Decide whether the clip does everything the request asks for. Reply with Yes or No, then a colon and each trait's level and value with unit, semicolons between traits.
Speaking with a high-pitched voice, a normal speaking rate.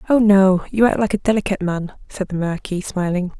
No: high, 195 Hz; fast, 210 wpm